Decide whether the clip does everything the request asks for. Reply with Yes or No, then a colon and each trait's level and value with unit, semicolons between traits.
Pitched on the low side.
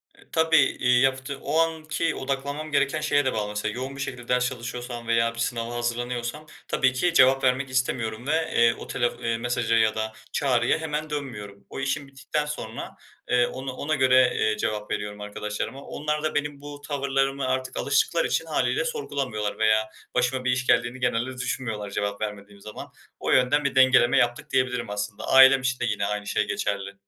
Yes: low, 125 Hz